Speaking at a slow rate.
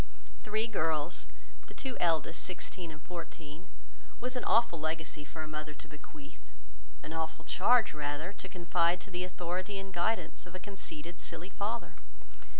No: average, 155 wpm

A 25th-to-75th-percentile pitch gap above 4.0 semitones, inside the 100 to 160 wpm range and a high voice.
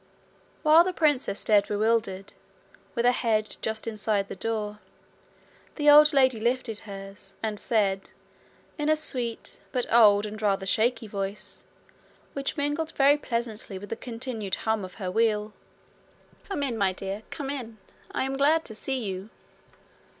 Yes: average, 4.5 semitones; average, 150 wpm; high, 225 Hz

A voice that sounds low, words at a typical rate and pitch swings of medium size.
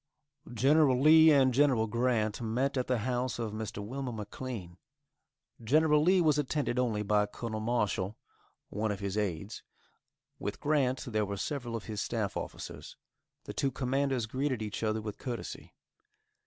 Yes: low, 120 Hz; average, 155 wpm; average, 4.1 semitones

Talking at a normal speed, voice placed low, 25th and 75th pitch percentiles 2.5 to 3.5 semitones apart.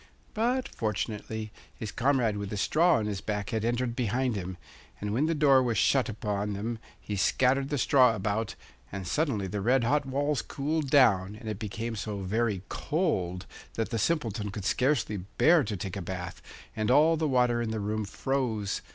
No: average, 185 wpm; low, 115 Hz; average, 4.6 semitones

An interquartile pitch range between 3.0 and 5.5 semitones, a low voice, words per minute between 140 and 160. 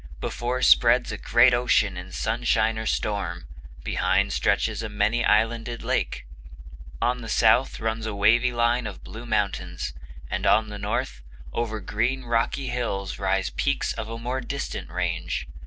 No: narrow, 2.6 semitones; low, 115 Hz; average, 155 wpm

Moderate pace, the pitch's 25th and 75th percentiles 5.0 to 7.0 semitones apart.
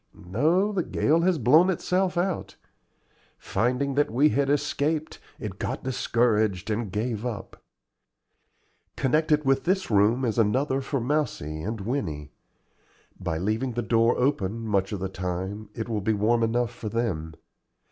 Yes: average, 145 wpm; average, 5.3 semitones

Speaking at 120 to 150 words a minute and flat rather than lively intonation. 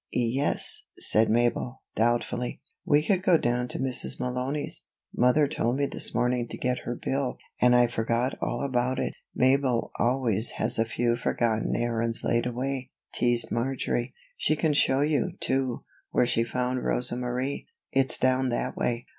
No: average, 165 wpm; narrow, 1.9 semitones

